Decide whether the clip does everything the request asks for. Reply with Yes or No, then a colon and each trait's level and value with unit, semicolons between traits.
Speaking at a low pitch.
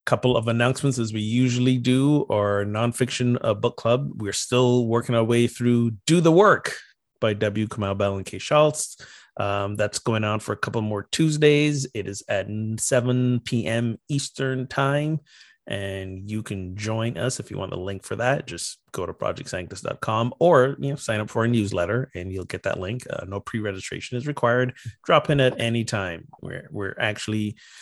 Yes: low, 115 Hz